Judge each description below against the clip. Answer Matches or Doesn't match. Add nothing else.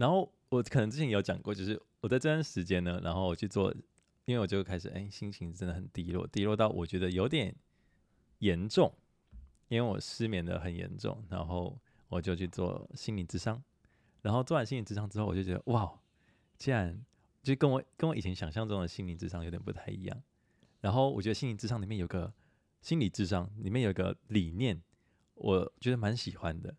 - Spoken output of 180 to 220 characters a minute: Doesn't match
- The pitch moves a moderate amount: Matches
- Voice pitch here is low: Matches